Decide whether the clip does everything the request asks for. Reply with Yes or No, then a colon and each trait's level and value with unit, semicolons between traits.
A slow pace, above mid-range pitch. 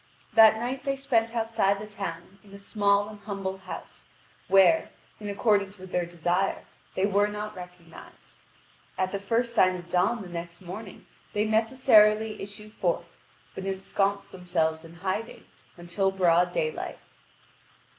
No: average, 145 wpm; high, 200 Hz